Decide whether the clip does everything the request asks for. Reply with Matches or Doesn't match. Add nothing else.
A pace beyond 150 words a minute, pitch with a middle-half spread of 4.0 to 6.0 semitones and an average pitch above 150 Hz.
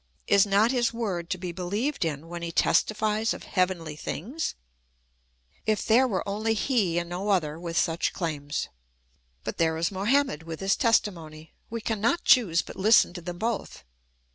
Matches